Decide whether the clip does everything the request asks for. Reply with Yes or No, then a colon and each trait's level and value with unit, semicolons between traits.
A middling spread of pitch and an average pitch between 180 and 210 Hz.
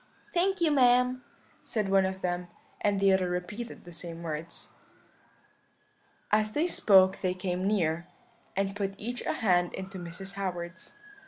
Yes: average, 3.2 semitones; high, 190 Hz